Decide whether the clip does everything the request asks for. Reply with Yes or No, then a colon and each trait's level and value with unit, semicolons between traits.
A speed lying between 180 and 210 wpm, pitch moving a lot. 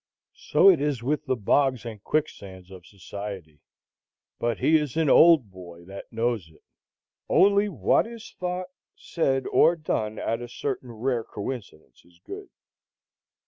No: average, 145 wpm; wide, 7.4 semitones